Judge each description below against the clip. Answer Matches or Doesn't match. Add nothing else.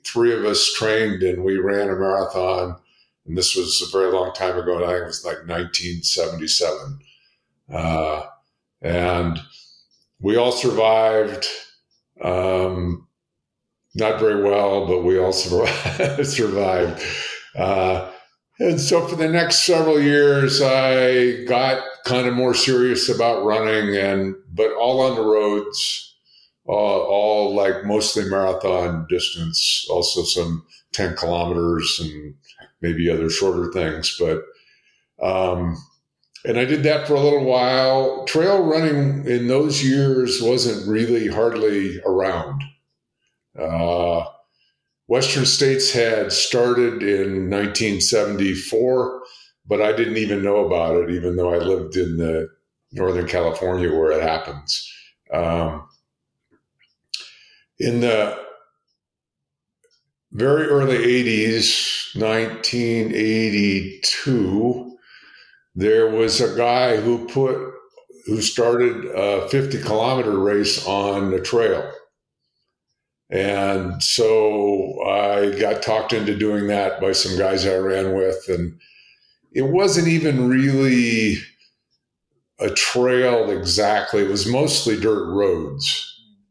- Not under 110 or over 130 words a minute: Matches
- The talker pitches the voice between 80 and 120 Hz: Matches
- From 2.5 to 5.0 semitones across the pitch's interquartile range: Doesn't match